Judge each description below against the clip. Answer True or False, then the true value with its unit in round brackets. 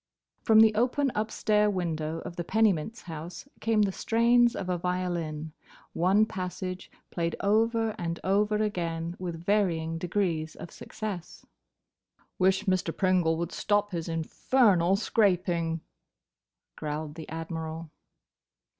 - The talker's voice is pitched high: False (180 Hz)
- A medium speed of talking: False (120 wpm)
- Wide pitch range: False (4.2 semitones)